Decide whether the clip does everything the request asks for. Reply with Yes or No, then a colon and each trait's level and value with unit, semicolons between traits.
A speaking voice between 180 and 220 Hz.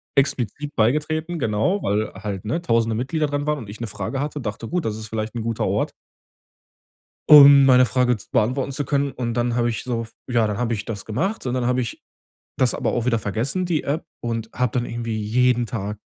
No: low, 120 Hz